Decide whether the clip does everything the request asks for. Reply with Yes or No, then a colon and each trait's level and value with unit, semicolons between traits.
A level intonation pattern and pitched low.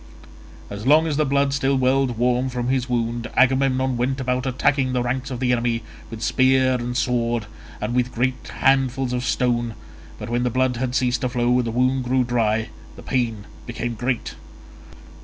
Yes: narrow, 1.6 semitones; low, 125 Hz